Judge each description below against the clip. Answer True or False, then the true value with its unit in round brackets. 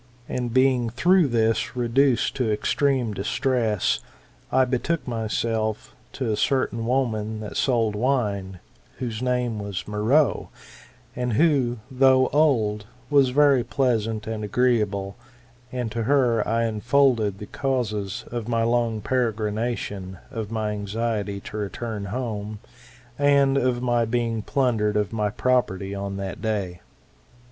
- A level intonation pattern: False (3.3 semitones)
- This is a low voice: True (115 Hz)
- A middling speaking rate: False (130 wpm)